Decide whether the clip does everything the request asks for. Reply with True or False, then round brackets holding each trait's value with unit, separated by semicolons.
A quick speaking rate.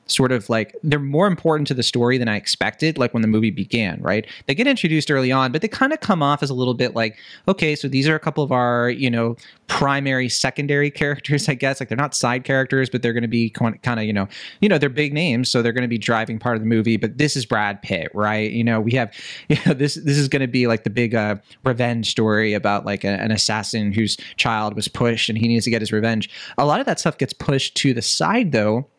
True (265 wpm)